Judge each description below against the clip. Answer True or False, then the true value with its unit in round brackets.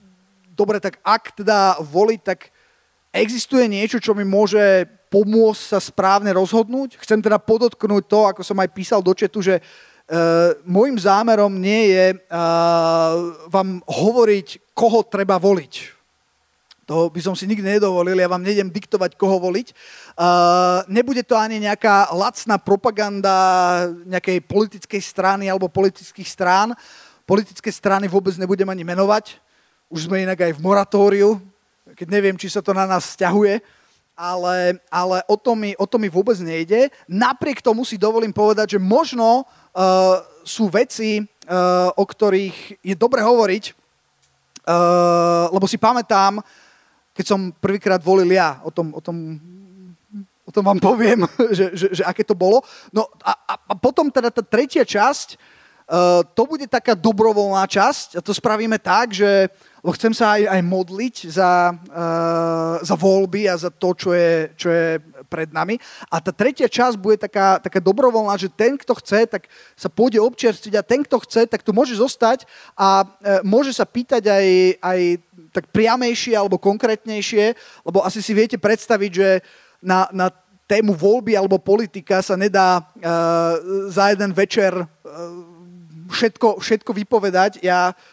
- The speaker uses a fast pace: False (155 wpm)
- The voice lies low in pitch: False (195 Hz)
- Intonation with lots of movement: False (2.9 semitones)